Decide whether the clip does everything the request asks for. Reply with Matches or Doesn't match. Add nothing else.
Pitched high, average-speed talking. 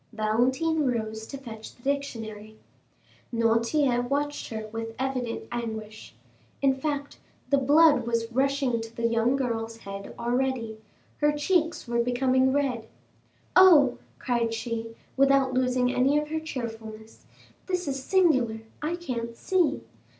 Doesn't match